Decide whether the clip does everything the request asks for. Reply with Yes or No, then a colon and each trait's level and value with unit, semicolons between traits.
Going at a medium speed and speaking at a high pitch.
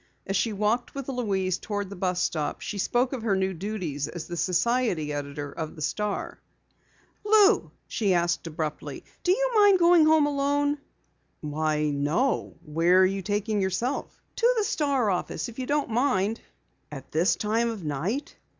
Yes: average, 165 wpm; high, 205 Hz